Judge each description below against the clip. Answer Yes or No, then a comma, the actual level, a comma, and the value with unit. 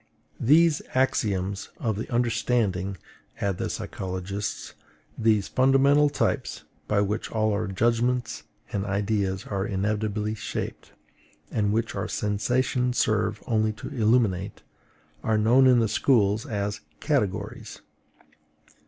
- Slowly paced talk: Yes, slow, 115 wpm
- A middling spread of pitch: Yes, average, 3.1 semitones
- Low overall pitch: Yes, low, 110 Hz